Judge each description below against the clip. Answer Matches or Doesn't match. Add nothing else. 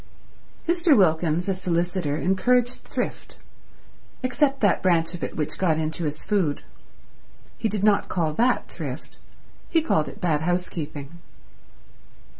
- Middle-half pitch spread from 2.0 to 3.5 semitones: Doesn't match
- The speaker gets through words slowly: Matches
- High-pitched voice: Doesn't match